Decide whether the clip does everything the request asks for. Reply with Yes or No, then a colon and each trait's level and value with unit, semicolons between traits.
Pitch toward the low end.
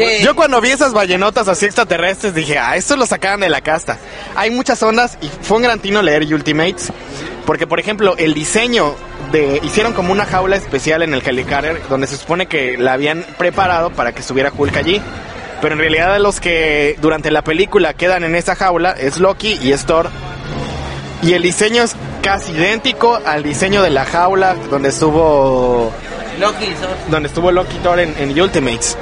No: medium, 170 Hz